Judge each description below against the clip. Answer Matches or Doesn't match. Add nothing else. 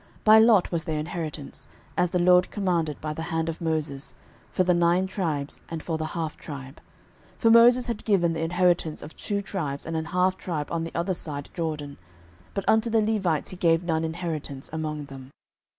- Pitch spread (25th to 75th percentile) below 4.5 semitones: Matches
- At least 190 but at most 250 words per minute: Matches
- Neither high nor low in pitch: Matches